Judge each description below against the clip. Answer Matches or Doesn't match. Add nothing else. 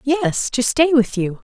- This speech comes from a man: Doesn't match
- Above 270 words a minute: Doesn't match